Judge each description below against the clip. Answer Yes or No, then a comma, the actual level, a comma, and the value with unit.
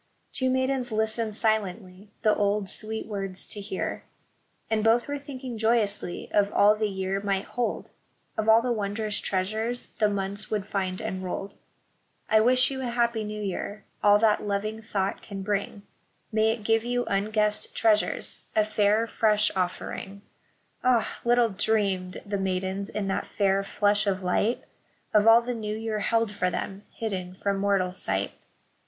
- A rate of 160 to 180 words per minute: Yes, average, 165 wpm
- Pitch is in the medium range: No, high, 210 Hz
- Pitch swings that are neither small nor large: No, narrow, 2.2 semitones